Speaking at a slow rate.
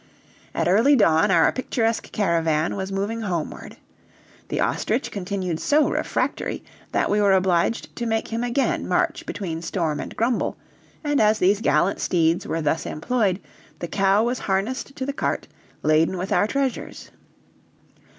No: average, 150 wpm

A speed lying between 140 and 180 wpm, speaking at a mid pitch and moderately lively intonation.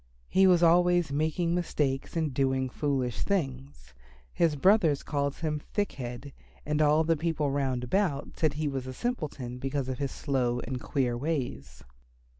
Yes: average, 160 wpm; medium, 145 Hz; average, 3.8 semitones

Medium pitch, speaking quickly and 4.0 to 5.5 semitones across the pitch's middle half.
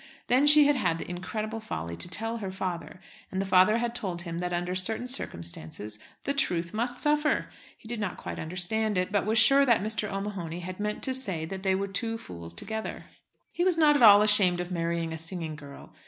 No: high, 195 Hz; fast, 215 wpm; average, 4.5 semitones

